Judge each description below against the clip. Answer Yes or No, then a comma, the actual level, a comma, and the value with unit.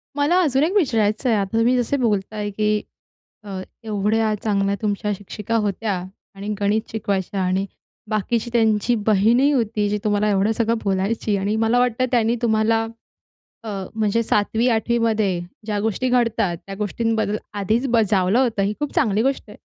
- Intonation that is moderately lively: No, narrow, 2.3 semitones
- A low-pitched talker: No, high, 220 Hz